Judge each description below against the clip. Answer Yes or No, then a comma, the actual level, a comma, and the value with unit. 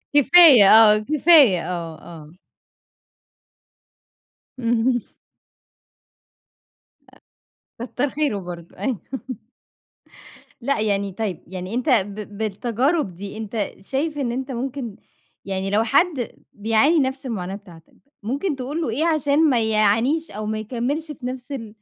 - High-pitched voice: Yes, high, 230 Hz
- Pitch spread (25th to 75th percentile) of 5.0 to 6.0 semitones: Yes, wide, 5.4 semitones